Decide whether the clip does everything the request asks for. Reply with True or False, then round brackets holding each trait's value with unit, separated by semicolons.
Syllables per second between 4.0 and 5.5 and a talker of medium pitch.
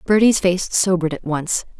True (5.1 syllables/s; 180 Hz)